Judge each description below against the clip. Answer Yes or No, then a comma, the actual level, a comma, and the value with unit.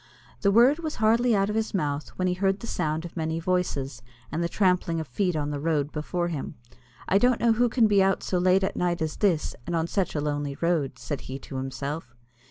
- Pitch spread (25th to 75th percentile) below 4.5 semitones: No, average, 4.9 semitones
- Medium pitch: Yes, medium, 175 Hz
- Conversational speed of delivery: No, fast, 235 wpm